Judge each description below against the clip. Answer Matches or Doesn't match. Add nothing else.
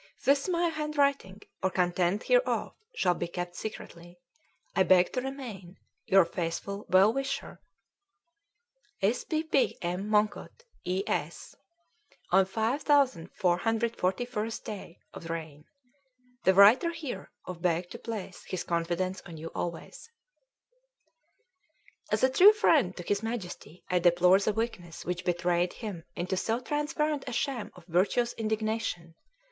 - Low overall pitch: Doesn't match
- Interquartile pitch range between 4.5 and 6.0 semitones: Matches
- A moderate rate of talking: Doesn't match